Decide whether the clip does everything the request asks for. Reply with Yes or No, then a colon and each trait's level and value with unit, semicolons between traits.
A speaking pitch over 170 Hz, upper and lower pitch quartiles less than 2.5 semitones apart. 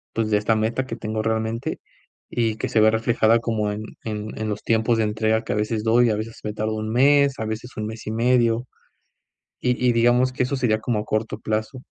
No: low, 110 Hz; narrow, 1.7 semitones